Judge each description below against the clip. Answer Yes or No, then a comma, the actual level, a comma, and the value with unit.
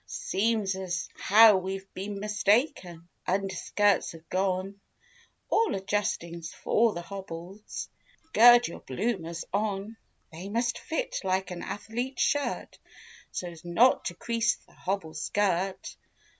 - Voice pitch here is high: Yes, high, 195 Hz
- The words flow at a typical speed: No, slow, 120 wpm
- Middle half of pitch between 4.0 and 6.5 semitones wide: No, average, 3.4 semitones